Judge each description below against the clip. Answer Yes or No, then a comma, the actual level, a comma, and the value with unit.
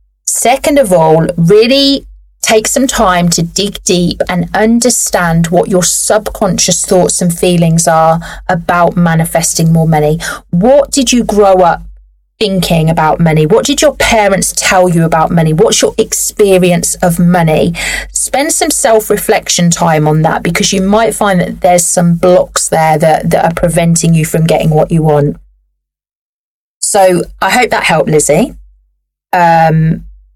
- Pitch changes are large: No, average, 4.0 semitones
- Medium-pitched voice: Yes, medium, 175 Hz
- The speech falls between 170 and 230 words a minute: No, average, 150 wpm